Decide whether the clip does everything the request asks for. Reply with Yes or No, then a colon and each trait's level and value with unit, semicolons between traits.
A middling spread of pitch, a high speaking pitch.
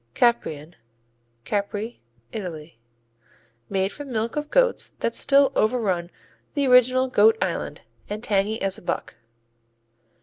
Yes: average, 4.9 semitones; high, 215 Hz